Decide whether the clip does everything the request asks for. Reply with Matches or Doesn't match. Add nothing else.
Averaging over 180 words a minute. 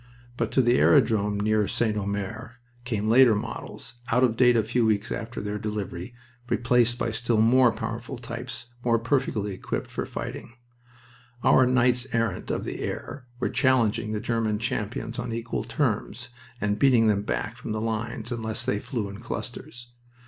Doesn't match